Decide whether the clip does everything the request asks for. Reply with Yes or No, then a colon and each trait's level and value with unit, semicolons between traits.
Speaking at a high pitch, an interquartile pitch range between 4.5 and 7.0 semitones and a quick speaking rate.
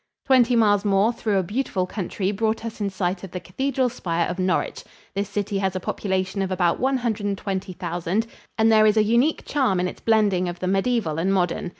No: high, 200 Hz; average, 3.3 semitones; fast, 220 wpm